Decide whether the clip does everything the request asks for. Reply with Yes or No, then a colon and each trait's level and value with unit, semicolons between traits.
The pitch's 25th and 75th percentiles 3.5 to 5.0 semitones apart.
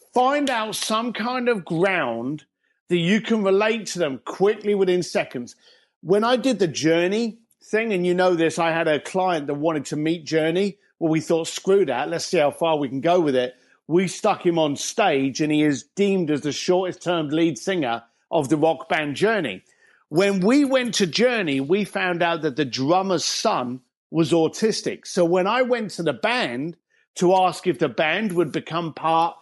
Yes: average, 4.2 semitones